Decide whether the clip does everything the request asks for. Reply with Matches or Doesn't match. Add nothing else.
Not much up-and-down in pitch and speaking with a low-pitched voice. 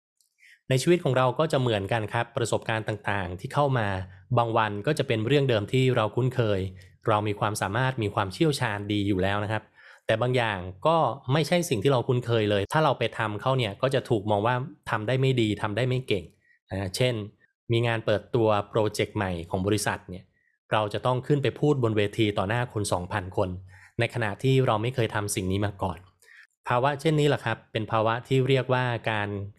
Doesn't match